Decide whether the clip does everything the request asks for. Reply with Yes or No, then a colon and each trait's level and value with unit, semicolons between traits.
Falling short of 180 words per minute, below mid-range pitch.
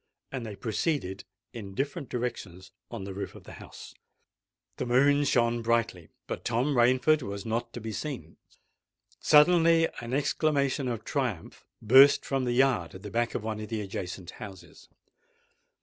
Yes: average, 160 wpm; low, 120 Hz